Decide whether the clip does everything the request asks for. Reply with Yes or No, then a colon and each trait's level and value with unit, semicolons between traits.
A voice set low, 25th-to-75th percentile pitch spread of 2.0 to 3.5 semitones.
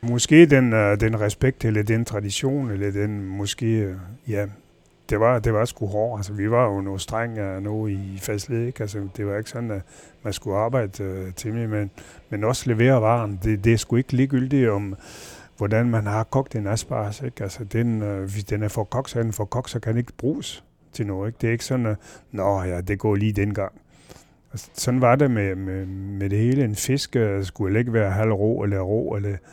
Yes: low, 110 Hz; average, 2.7 semitones